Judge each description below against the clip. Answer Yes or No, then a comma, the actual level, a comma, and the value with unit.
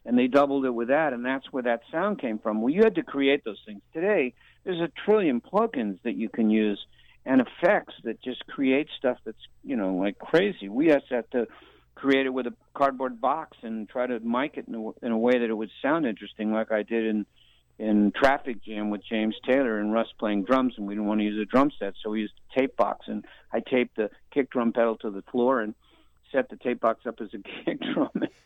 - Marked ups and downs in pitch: No, average, 3.8 semitones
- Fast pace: Yes, fast, 240 wpm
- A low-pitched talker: Yes, low, 120 Hz